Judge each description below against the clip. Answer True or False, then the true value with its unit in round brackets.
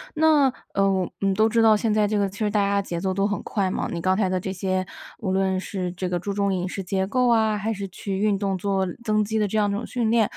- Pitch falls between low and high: False (200 Hz)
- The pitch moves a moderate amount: False (2.2 semitones)